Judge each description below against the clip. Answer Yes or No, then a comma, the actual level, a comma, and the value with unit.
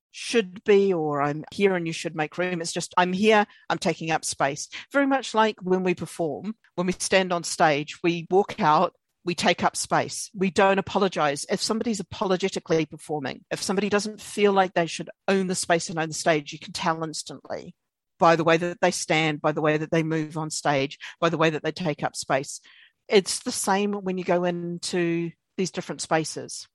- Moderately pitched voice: Yes, medium, 175 Hz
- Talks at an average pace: No, fast, 210 wpm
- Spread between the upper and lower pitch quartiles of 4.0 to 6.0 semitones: No, average, 3.5 semitones